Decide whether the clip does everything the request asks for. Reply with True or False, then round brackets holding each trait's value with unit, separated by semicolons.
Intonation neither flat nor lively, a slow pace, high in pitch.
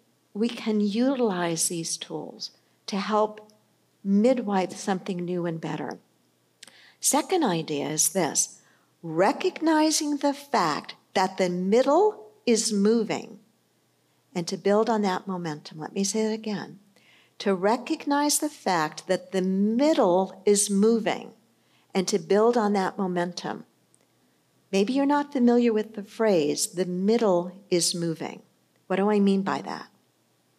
True (4.1 semitones; 130 wpm; 200 Hz)